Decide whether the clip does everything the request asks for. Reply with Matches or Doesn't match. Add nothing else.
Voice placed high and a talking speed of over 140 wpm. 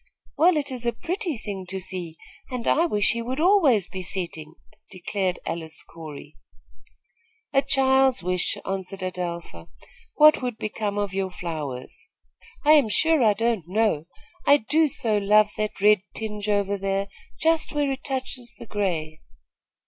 Matches